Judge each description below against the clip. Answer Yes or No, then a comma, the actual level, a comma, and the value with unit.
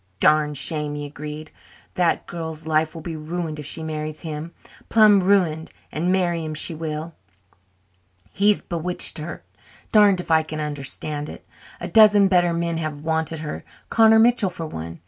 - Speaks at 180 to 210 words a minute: No, average, 165 wpm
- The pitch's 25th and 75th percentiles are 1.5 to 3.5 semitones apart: Yes, narrow, 2.6 semitones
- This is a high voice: No, medium, 160 Hz